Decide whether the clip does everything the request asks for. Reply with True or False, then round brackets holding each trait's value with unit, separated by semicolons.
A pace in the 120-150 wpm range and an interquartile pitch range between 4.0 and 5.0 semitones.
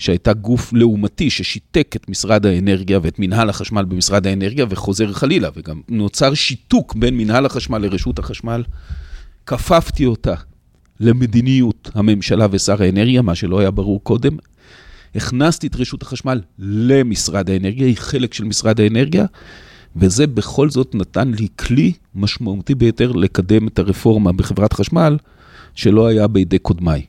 True (135 wpm; 4.3 semitones)